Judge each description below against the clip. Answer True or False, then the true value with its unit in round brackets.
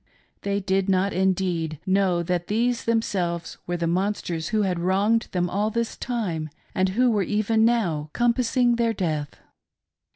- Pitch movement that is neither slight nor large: True (4.3 semitones)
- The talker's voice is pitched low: False (195 Hz)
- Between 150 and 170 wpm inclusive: True (155 wpm)